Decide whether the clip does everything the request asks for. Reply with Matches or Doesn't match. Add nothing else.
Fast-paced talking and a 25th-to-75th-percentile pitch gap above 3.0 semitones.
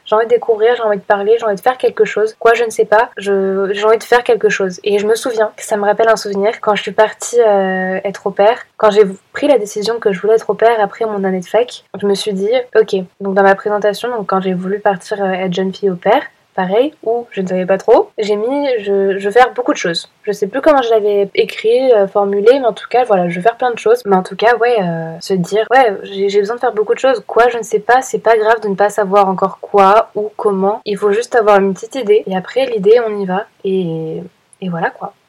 Doesn't match